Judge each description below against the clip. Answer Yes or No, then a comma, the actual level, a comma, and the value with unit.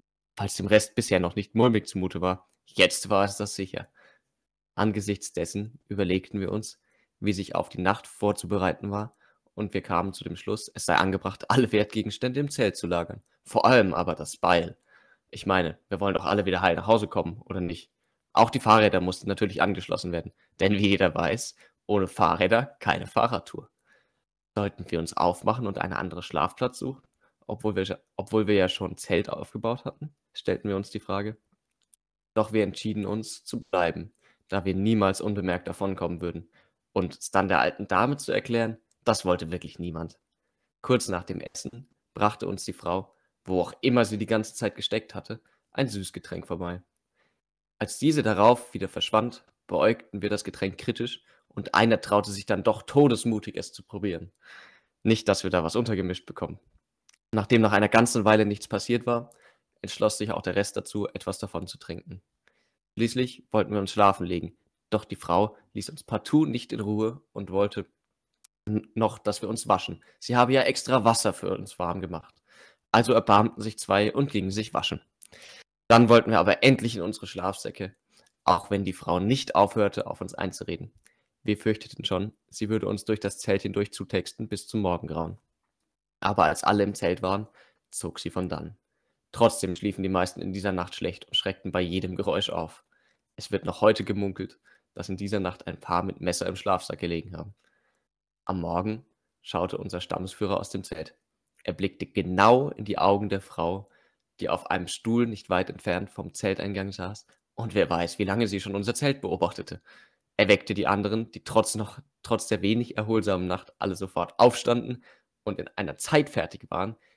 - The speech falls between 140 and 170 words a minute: No, average, 180 wpm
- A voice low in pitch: Yes, low, 100 Hz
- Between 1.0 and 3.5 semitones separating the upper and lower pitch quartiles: Yes, average, 2.8 semitones